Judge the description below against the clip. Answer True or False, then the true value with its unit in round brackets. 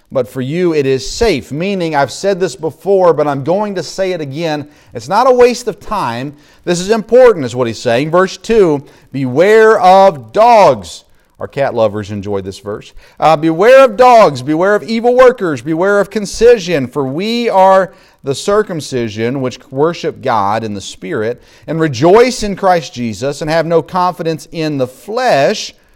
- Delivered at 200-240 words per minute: False (175 wpm)